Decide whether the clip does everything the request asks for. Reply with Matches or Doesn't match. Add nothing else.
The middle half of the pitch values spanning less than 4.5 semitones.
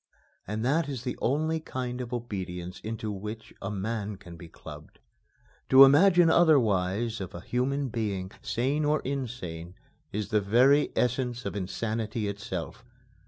Doesn't match